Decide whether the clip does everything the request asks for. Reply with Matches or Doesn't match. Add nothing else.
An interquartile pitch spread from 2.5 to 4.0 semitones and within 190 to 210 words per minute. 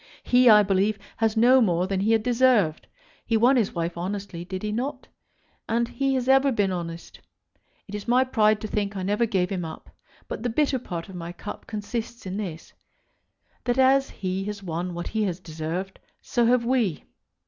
Doesn't match